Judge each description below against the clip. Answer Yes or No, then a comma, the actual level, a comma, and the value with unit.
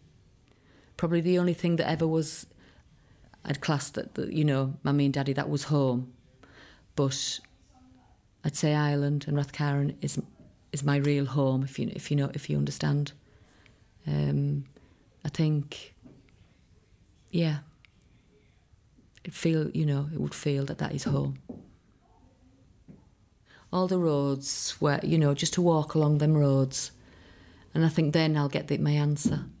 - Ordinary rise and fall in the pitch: Yes, average, 4.4 semitones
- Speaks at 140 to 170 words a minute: Yes, average, 150 wpm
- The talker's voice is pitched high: No, medium, 140 Hz